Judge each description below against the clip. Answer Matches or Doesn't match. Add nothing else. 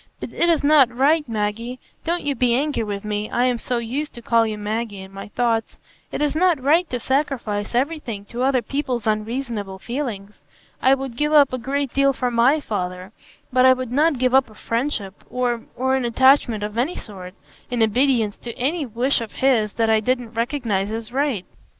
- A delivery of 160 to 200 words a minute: Matches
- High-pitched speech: Matches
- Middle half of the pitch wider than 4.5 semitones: Doesn't match